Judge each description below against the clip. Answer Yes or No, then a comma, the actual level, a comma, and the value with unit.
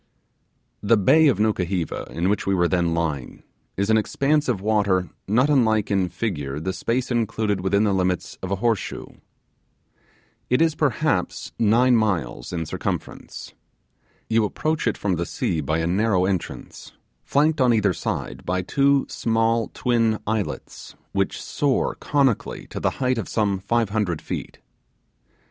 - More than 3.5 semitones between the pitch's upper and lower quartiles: Yes, average, 4.4 semitones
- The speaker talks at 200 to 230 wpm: No, average, 155 wpm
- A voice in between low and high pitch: No, low, 105 Hz